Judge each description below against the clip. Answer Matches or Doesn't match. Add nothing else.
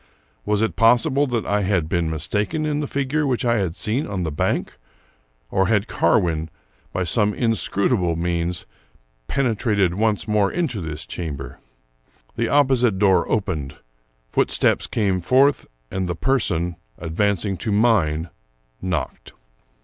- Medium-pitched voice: Doesn't match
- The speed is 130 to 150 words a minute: Matches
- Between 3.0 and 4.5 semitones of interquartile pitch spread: Doesn't match